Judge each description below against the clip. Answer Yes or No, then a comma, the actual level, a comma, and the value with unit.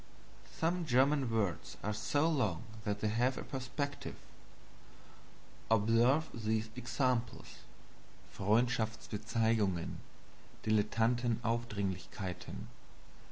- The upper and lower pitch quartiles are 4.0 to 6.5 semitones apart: No, average, 3.0 semitones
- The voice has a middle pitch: No, low, 115 Hz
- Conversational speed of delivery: No, slow, 70 wpm